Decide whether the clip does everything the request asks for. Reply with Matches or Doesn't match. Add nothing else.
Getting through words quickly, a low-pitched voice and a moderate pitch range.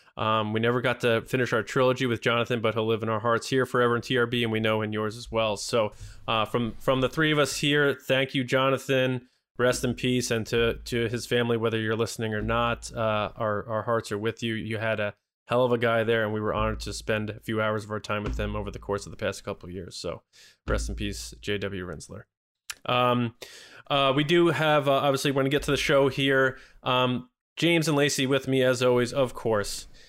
Matches